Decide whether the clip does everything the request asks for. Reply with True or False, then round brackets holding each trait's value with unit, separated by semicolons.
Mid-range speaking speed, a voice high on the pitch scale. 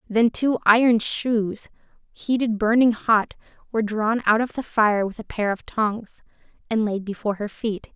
True (175 wpm; 220 Hz)